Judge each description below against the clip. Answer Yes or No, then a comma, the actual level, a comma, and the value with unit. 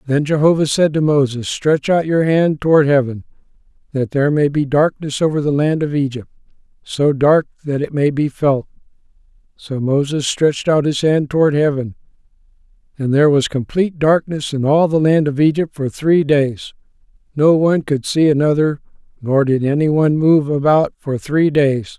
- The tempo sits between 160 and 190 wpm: Yes, average, 175 wpm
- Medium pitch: Yes, medium, 145 Hz